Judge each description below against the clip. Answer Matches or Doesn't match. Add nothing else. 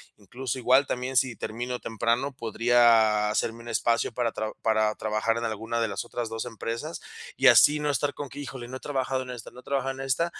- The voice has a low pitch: Matches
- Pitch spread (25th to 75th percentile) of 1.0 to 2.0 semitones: Doesn't match